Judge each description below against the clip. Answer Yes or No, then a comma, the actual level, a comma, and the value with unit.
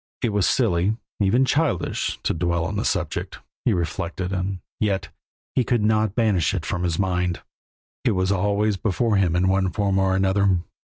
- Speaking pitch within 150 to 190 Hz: No, very low, 95 Hz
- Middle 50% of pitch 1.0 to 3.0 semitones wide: Yes, narrow, 2.6 semitones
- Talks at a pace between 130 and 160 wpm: No, average, 175 wpm